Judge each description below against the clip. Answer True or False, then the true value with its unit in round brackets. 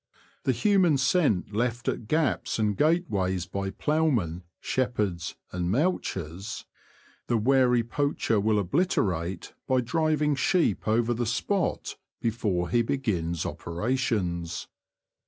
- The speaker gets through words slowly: True (110 wpm)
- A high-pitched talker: False (115 Hz)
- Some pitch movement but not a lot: False (6.9 semitones)